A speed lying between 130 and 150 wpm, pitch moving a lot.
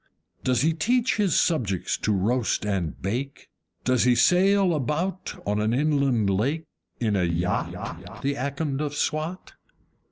Yes: average, 140 wpm; wide, 7.0 semitones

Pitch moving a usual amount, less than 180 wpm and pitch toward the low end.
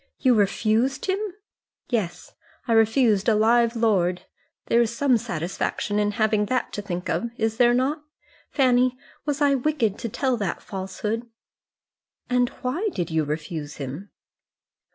No: average, 4.3 semitones; average, 145 wpm; high, 225 Hz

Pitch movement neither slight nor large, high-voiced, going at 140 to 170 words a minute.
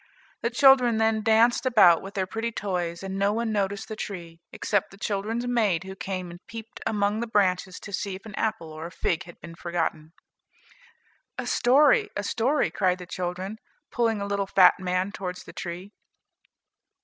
No: average, 3.6 semitones; high, 200 Hz; average, 185 wpm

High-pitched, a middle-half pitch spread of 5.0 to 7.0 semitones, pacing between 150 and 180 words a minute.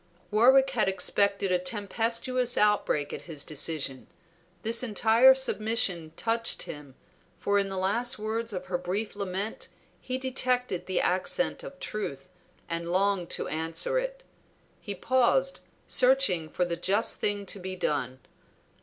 No: high, 205 Hz; average, 5.3 semitones; average, 140 wpm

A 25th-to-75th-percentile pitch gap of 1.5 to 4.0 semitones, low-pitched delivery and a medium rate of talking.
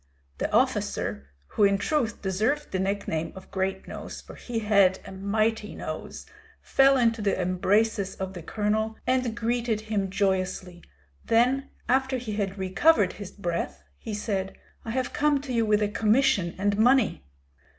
No: average, 3.6 semitones; high, 210 Hz; average, 160 wpm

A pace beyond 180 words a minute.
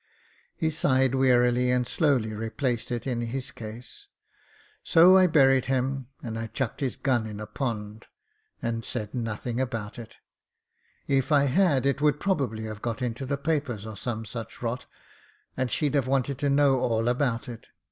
No: average, 170 wpm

